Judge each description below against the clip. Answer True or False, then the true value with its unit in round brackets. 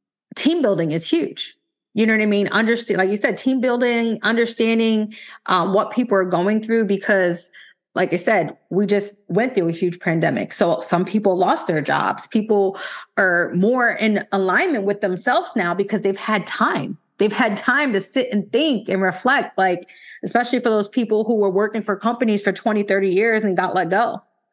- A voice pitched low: False (210 Hz)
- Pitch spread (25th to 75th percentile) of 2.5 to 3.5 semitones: True (2.9 semitones)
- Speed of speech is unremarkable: True (190 wpm)